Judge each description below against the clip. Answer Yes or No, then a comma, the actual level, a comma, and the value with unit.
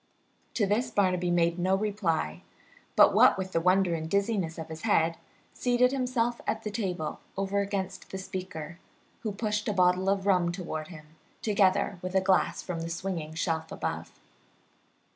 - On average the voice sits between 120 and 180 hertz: No, high, 190 Hz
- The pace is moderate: Yes, average, 165 wpm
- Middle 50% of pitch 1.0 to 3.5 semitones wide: Yes, average, 3.2 semitones